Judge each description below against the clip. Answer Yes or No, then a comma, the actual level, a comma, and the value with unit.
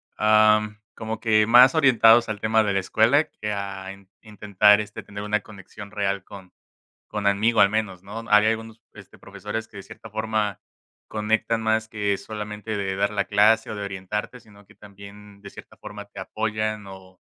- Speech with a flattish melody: Yes, narrow, 1.5 semitones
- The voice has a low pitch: Yes, low, 105 Hz